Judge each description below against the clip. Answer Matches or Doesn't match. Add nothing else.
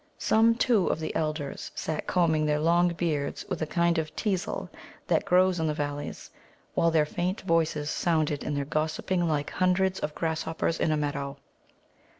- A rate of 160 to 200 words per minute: Matches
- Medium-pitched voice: Matches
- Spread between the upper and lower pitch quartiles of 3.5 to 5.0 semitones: Doesn't match